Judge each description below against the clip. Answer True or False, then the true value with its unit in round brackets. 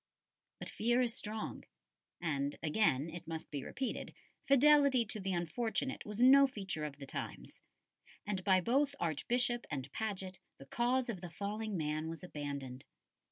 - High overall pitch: True (195 Hz)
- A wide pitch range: True (7.4 semitones)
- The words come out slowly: False (155 wpm)